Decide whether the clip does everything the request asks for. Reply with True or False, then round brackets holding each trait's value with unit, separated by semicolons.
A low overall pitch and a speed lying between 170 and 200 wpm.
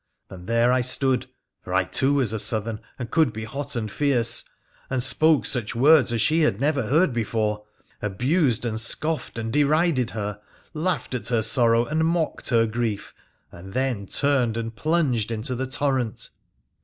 True (120 Hz; 180 wpm)